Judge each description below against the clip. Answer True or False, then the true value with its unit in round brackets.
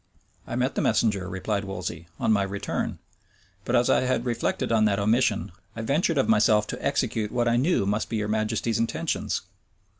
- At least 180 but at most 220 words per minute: True (185 wpm)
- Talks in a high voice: False (110 Hz)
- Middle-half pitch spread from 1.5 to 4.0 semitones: True (2.9 semitones)